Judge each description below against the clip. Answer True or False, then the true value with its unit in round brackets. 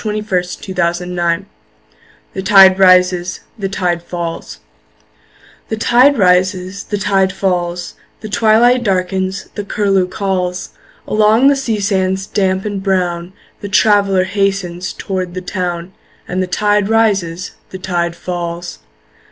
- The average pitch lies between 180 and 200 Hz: True (190 Hz)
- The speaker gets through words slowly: True (125 wpm)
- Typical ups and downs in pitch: False (2.1 semitones)